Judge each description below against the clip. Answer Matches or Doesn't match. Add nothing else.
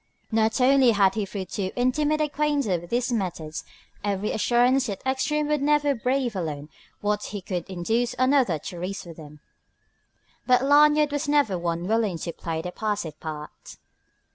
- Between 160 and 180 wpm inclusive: Matches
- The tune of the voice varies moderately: Doesn't match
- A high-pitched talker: Matches